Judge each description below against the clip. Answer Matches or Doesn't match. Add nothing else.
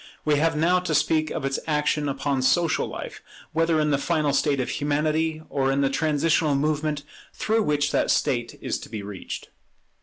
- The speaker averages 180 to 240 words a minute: Matches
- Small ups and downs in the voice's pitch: Matches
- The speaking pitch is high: Doesn't match